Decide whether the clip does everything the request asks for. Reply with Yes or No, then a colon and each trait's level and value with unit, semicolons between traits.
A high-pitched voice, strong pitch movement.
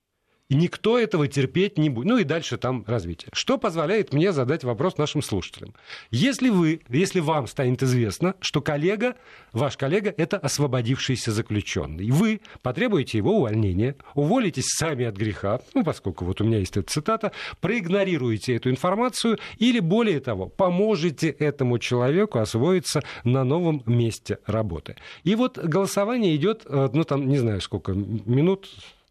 No: medium, 150 Hz; wide, 8.3 semitones